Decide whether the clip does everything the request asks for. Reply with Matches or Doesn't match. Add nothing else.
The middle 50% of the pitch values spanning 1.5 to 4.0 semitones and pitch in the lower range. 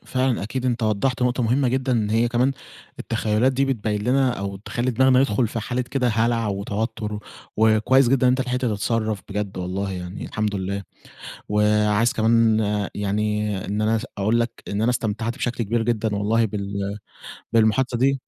Matches